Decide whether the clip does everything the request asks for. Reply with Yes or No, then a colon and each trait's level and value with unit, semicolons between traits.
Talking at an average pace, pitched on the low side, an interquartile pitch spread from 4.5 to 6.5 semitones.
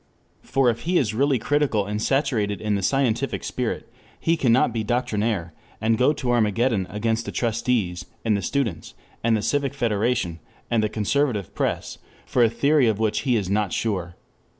No: average, 175 wpm; low, 115 Hz; average, 3.5 semitones